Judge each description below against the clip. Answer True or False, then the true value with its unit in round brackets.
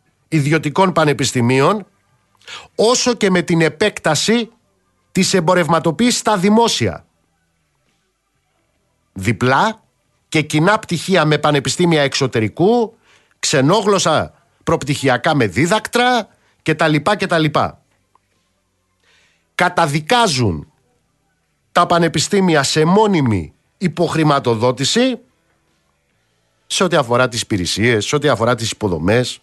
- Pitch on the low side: False (155 Hz)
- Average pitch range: False (7.6 semitones)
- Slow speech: True (85 wpm)